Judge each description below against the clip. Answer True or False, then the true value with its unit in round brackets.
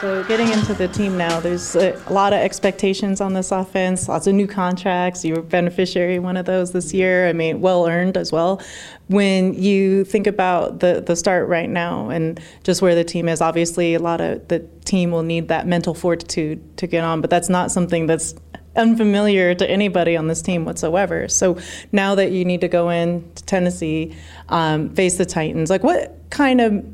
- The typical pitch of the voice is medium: True (180 Hz)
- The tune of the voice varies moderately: False (2.2 semitones)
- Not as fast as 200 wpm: False (205 wpm)